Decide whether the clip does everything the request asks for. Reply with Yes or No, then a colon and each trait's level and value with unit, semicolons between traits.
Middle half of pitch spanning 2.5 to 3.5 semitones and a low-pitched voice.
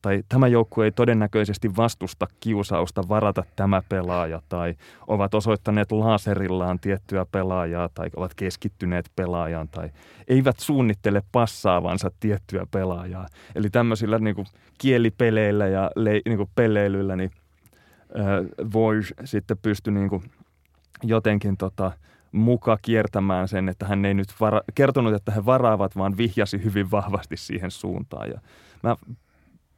Yes: average, 2.9 semitones; low, 100 Hz